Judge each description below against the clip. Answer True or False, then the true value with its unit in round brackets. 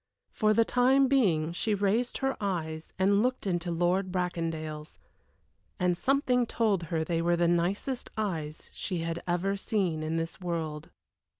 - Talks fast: False (155 wpm)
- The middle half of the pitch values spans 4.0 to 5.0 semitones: True (4.5 semitones)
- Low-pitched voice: False (180 Hz)